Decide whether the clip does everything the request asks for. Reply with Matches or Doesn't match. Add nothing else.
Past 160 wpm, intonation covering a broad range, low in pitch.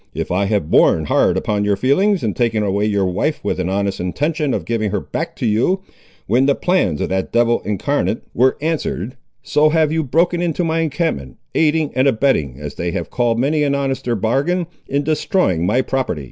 Matches